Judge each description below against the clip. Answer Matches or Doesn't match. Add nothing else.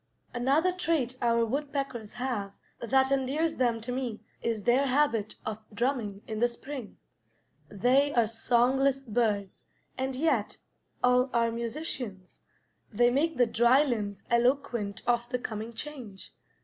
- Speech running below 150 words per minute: Matches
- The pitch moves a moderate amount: Matches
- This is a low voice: Doesn't match